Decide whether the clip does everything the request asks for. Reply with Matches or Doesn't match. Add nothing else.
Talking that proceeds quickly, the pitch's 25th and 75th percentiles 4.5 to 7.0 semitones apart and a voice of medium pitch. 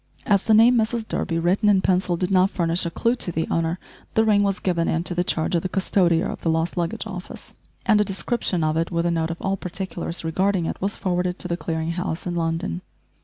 Doesn't match